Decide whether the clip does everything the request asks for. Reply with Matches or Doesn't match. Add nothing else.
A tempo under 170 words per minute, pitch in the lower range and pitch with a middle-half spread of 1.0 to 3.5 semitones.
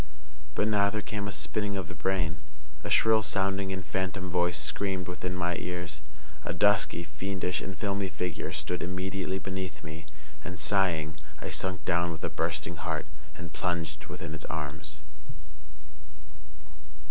Matches